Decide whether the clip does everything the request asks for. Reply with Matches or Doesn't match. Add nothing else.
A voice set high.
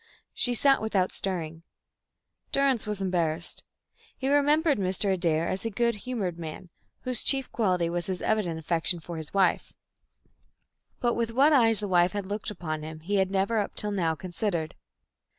Matches